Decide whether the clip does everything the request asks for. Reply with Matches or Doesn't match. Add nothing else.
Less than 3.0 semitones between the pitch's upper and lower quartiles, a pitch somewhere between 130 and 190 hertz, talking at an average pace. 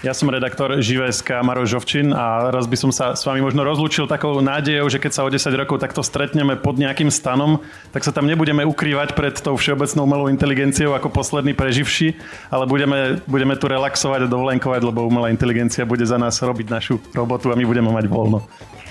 Doesn't match